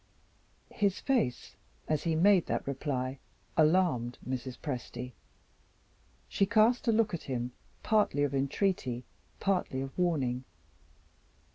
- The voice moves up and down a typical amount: No, wide, 7.0 semitones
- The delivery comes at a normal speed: No, slow, 115 wpm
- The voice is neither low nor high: Yes, medium, 145 Hz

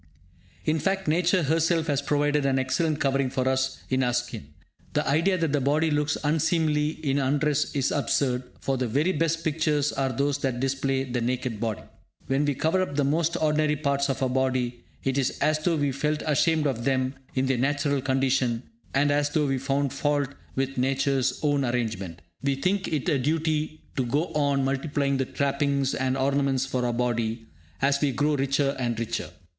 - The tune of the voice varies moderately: No, narrow, 2.3 semitones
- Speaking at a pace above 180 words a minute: Yes, average, 190 wpm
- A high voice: No, medium, 140 Hz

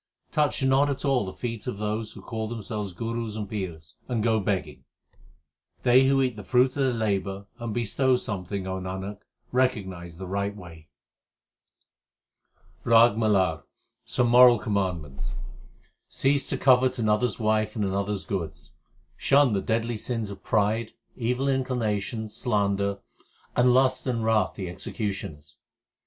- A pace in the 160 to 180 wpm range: No, average, 150 wpm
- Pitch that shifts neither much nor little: Yes, average, 4.1 semitones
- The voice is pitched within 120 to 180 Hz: No, low, 110 Hz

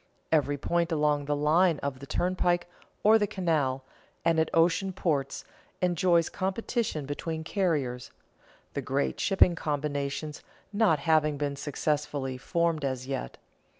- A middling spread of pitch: Yes, average, 3.6 semitones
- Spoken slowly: Yes, slow, 130 wpm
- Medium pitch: Yes, medium, 155 Hz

